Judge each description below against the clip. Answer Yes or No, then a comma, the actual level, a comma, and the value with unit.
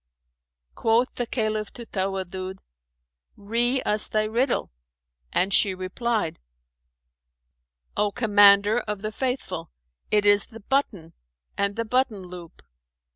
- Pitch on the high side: Yes, high, 210 Hz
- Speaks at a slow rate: Yes, slow, 115 wpm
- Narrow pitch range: No, average, 3.2 semitones